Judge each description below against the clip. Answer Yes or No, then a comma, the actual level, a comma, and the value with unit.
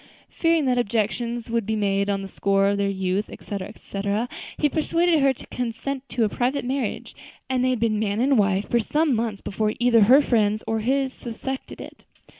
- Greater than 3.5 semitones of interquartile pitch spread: Yes, average, 4.3 semitones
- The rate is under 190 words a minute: No, average, 200 wpm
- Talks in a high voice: Yes, high, 230 Hz